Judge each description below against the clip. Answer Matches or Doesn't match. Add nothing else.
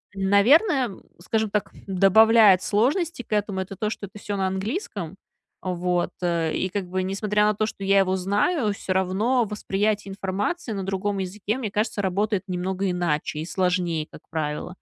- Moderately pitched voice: Doesn't match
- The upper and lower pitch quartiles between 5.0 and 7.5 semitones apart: Doesn't match